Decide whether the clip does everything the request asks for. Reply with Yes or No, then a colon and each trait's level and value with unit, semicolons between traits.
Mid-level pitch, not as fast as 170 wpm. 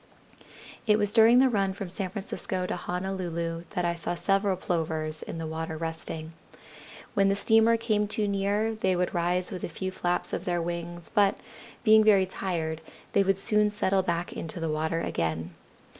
No: medium, 180 Hz; average, 180 wpm